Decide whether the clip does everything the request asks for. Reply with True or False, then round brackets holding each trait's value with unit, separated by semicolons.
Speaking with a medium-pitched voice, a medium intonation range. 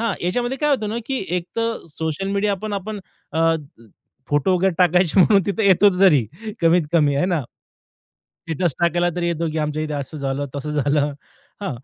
True (175 Hz; 4.6 semitones)